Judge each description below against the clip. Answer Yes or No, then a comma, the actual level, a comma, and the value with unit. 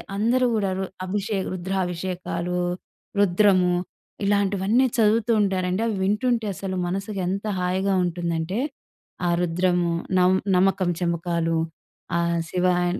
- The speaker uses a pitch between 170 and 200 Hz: Yes, medium, 185 Hz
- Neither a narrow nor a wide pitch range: No, narrow, 2.2 semitones